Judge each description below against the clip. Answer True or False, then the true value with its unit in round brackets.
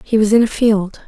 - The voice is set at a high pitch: True (215 Hz)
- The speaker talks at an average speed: False (280 wpm)